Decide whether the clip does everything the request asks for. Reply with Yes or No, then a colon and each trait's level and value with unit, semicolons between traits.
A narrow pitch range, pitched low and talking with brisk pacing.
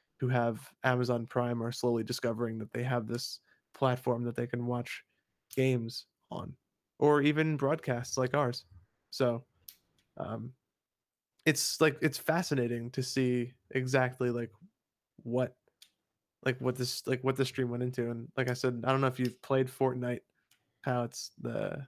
No: narrow, 1.8 semitones; low, 125 Hz; average, 155 wpm